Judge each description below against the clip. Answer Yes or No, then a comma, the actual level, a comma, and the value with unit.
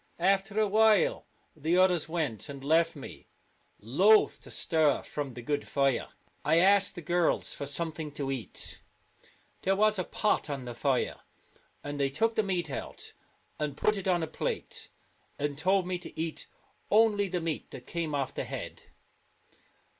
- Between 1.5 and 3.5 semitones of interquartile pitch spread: No, average, 5.0 semitones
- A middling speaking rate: Yes, average, 170 wpm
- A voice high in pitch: No, medium, 165 Hz